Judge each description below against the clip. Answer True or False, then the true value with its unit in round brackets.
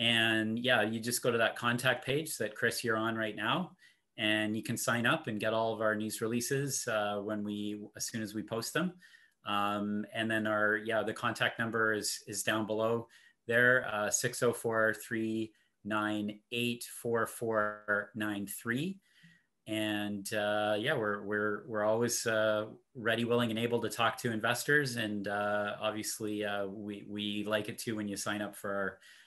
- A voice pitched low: True (110 Hz)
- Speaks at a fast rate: False (170 wpm)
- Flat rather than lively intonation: True (1.9 semitones)